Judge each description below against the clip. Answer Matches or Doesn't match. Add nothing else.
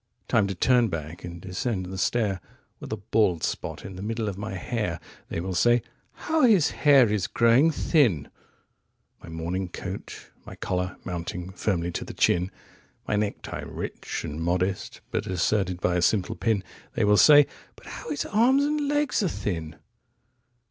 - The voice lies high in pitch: Doesn't match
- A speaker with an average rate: Matches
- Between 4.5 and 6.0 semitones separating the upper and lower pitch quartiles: Matches